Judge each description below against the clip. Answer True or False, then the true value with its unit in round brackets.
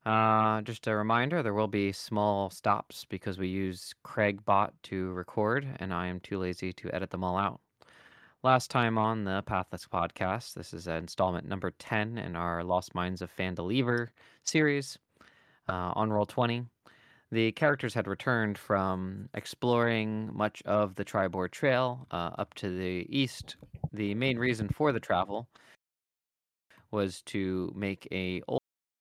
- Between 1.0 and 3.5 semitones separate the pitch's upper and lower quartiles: False (3.9 semitones)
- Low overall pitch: True (105 Hz)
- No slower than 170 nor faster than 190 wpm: False (155 wpm)